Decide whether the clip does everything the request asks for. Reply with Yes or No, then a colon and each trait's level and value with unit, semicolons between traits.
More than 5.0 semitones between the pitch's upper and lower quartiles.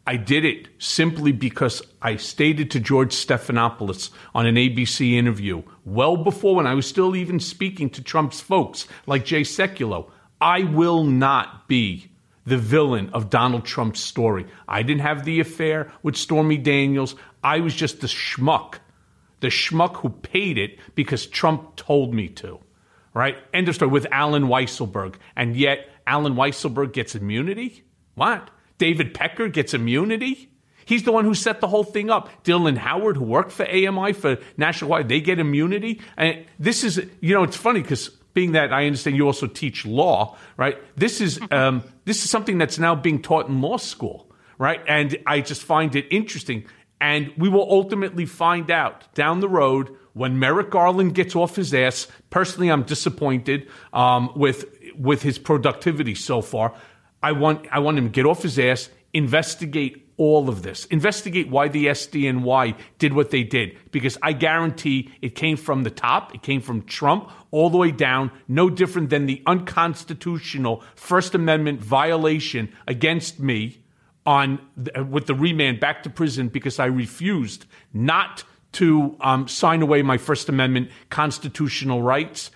No: average, 4.2 semitones